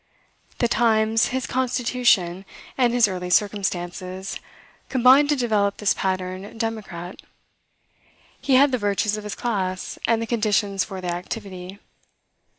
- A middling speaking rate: No, slow, 130 wpm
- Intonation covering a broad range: No, average, 4.2 semitones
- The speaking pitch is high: Yes, high, 210 Hz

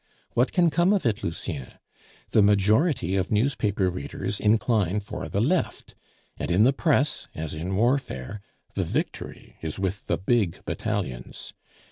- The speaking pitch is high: No, low, 105 Hz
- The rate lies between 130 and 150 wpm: Yes, average, 145 wpm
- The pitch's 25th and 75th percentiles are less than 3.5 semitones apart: No, average, 5.3 semitones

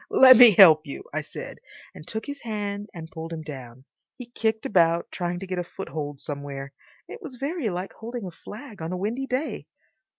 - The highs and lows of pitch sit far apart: Yes, wide, 6.5 semitones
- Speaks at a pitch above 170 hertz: Yes, high, 190 Hz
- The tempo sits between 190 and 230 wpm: Yes, average, 200 wpm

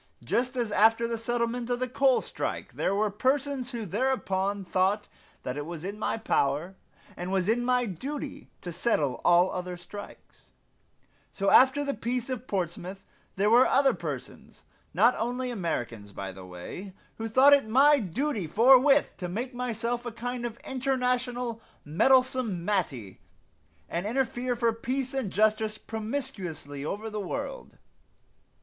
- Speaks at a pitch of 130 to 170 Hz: No, high, 225 Hz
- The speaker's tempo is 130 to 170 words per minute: Yes, average, 150 wpm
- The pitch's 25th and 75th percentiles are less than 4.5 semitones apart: No, average, 5.1 semitones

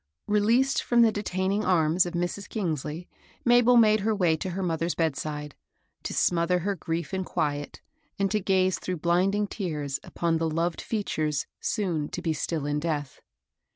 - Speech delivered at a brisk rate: No, average, 165 wpm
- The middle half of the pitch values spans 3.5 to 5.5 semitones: Yes, average, 4.2 semitones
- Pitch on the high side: No, medium, 175 Hz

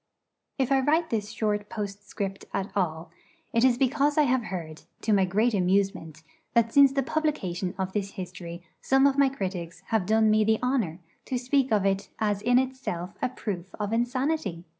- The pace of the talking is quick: No, average, 185 wpm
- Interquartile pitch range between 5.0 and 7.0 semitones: Yes, average, 5.3 semitones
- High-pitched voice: Yes, high, 215 Hz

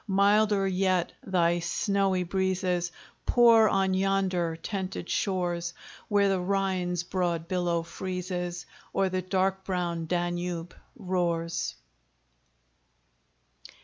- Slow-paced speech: Yes, slow, 95 wpm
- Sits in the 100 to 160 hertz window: No, medium, 185 Hz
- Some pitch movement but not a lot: No, narrow, 1.8 semitones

